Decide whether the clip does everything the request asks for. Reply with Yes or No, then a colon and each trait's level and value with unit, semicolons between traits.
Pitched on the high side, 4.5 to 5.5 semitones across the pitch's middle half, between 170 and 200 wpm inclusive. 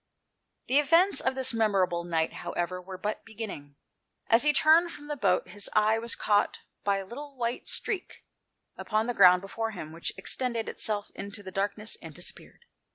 Yes: high, 215 Hz; average, 4.9 semitones; average, 175 wpm